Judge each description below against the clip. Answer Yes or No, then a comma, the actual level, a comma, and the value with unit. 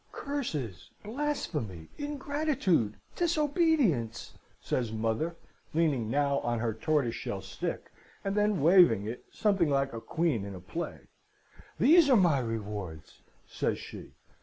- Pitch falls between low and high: Yes, medium, 150 Hz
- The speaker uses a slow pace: Yes, slow, 120 wpm